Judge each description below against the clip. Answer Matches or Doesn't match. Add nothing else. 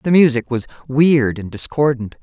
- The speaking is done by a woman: Matches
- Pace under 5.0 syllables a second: Matches